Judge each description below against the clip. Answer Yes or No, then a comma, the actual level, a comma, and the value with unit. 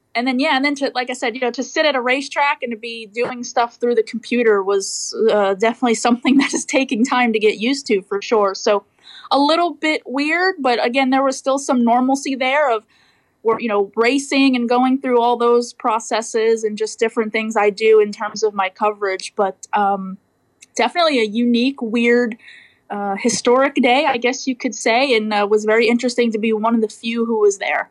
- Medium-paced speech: No, fast, 215 wpm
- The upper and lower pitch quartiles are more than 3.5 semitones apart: No, average, 3.2 semitones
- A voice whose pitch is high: Yes, high, 240 Hz